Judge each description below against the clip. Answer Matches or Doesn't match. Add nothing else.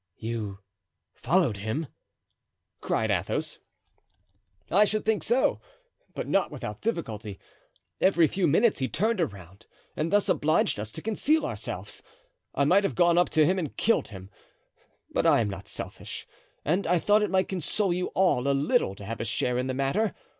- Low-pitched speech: Doesn't match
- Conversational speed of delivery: Matches